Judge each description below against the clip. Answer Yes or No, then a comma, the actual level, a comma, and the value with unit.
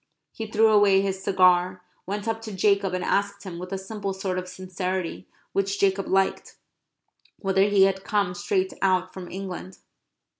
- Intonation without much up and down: Yes, narrow, 1.4 semitones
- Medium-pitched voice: No, high, 195 Hz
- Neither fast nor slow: Yes, average, 165 wpm